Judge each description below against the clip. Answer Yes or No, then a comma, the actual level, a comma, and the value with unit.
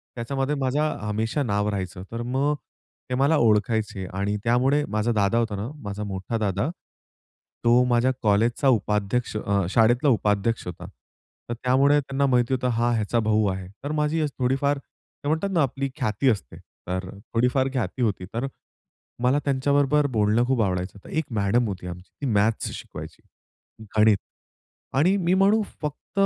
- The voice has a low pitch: Yes, low, 120 Hz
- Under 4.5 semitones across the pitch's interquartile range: No, average, 4.8 semitones